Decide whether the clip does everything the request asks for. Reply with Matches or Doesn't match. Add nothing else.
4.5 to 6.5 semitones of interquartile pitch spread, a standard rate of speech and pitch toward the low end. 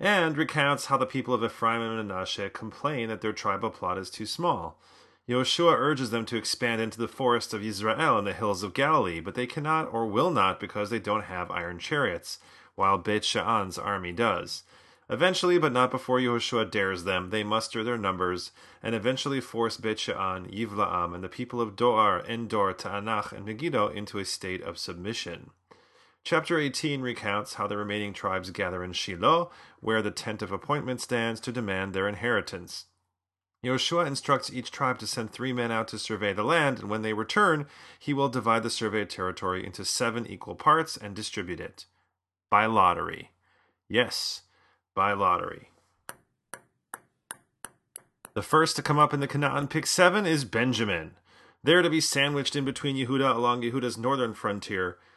Matches